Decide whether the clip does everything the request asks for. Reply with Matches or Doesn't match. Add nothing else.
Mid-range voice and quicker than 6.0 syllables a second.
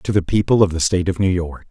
Doesn't match